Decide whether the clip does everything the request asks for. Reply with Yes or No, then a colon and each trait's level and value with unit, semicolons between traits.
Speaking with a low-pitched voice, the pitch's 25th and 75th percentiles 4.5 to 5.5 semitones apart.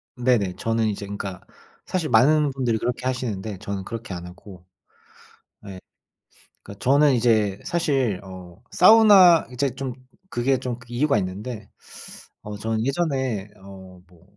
Yes: low, 115 Hz; average, 5.2 semitones